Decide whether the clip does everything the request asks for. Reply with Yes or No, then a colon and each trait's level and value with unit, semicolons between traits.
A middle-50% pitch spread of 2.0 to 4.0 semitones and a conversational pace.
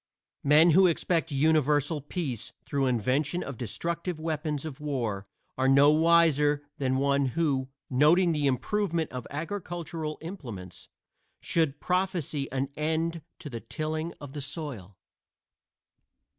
No: average, 3.4 semitones; slow, 125 wpm